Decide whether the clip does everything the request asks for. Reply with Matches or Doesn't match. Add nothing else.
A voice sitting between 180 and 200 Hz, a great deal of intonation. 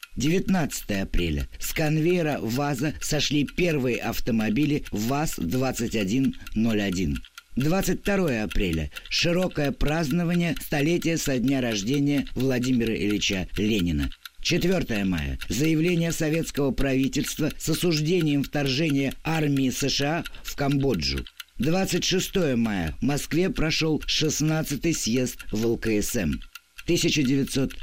Doesn't match